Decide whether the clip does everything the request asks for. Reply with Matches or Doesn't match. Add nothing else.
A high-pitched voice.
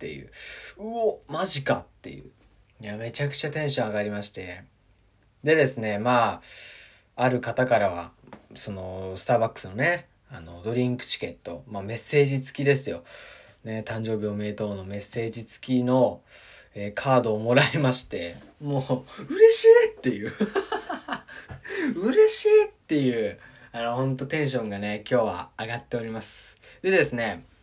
Doesn't match